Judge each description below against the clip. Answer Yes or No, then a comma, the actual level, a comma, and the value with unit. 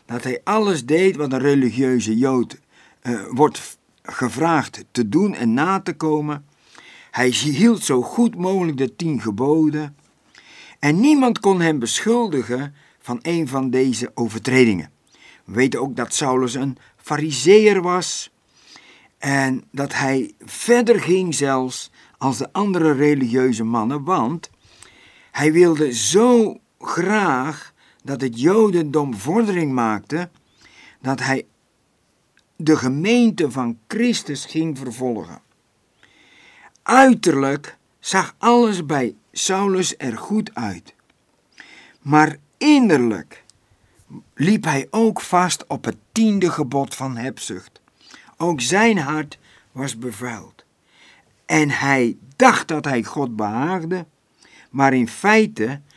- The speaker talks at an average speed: No, slow, 115 wpm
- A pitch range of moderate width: No, wide, 6.2 semitones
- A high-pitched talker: No, medium, 150 Hz